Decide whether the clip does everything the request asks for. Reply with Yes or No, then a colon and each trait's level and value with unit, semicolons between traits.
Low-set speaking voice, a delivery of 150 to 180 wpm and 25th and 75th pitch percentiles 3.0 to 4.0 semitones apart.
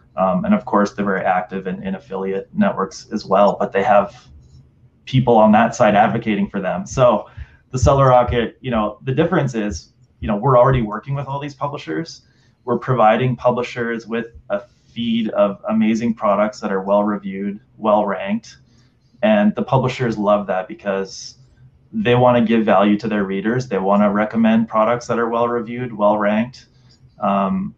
Yes: low, 115 Hz; average, 175 wpm; average, 3.7 semitones